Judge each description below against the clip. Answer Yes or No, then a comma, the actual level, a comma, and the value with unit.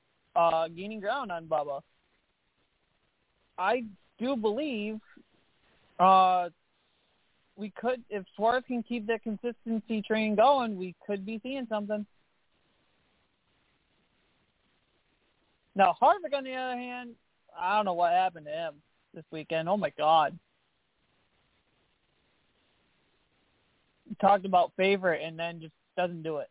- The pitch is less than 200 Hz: No, high, 210 Hz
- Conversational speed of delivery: No, slow, 120 wpm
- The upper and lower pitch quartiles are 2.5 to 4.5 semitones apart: No, average, 5.3 semitones